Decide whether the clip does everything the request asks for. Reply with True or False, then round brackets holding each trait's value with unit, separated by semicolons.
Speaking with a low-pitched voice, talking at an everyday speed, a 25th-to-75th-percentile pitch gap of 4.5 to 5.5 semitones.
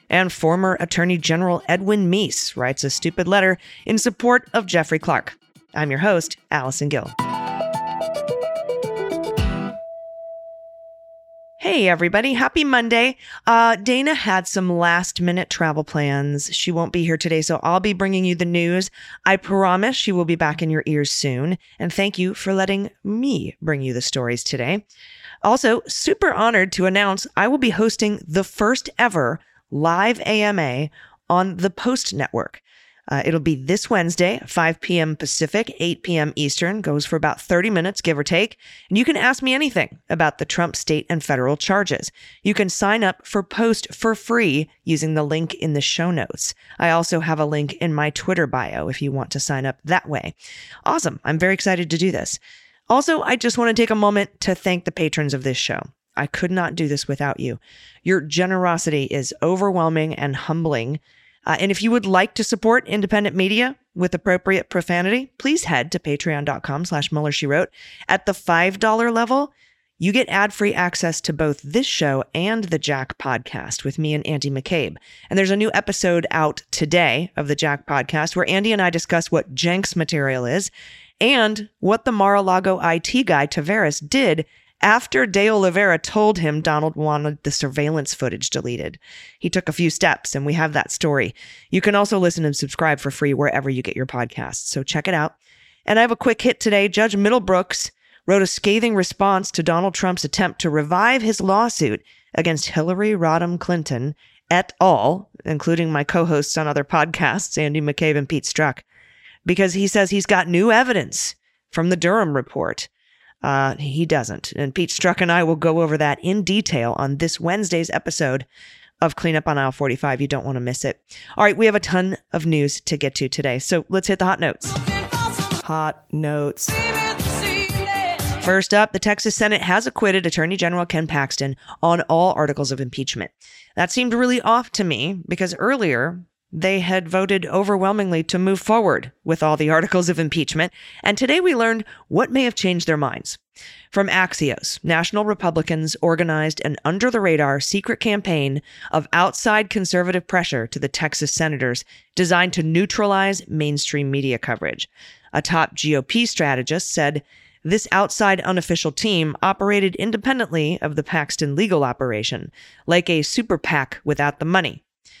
False (175 Hz; 175 wpm; 5.0 semitones)